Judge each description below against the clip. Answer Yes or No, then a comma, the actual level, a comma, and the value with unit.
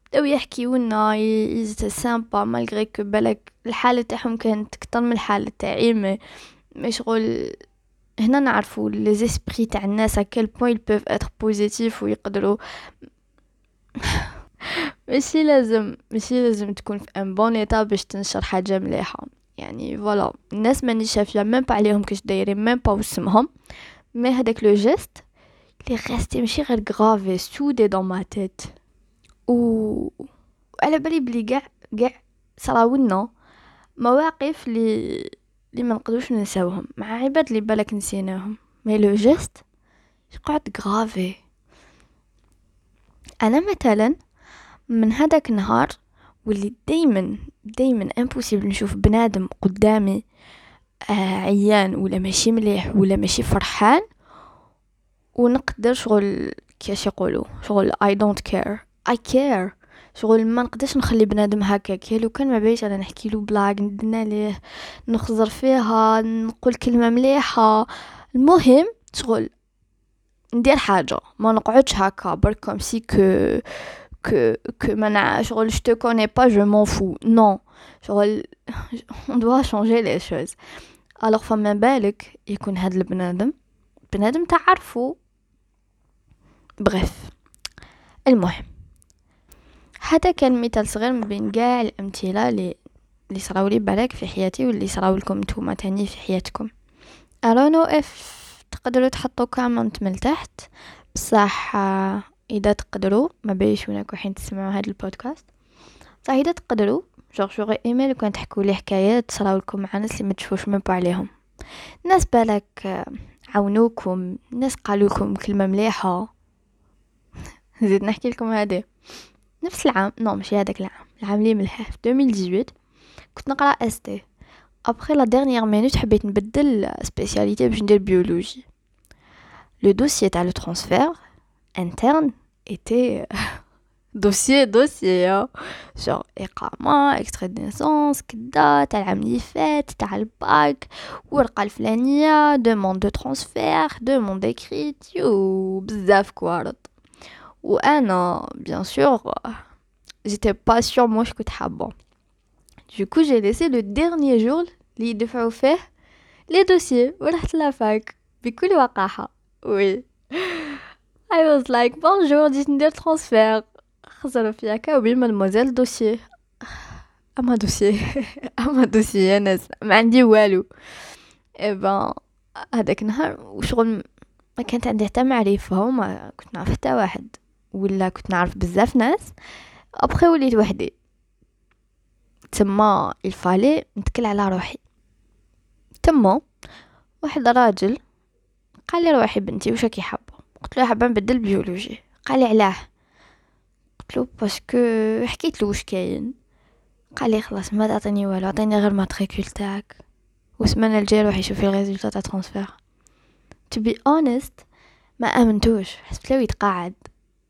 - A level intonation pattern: No, average, 3.9 semitones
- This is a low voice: No, high, 220 Hz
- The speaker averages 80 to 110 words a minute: No, average, 120 wpm